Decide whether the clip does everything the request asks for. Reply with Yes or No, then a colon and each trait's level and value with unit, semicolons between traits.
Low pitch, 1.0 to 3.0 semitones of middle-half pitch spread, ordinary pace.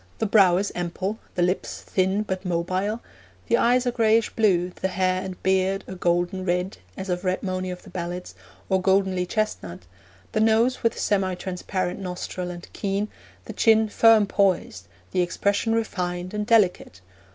No: high, 190 Hz; average, 2.7 semitones; average, 165 wpm